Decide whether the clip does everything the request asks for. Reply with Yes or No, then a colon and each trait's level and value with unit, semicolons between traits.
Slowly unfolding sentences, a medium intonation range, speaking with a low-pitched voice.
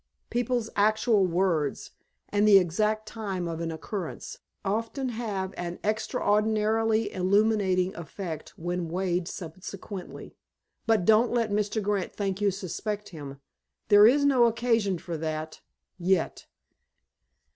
No: slow, 115 wpm; average, 3.5 semitones; high, 200 Hz